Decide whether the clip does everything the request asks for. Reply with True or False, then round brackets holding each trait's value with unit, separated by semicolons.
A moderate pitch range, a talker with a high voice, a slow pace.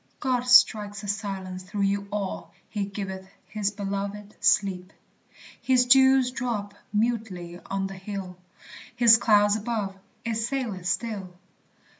True (3.0 semitones; 205 Hz; 125 wpm)